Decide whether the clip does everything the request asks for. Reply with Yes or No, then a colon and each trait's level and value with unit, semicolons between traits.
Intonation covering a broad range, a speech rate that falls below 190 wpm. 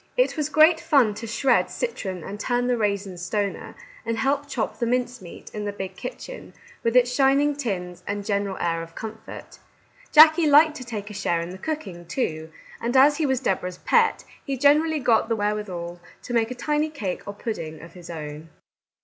No: wide, 6.8 semitones; average, 195 wpm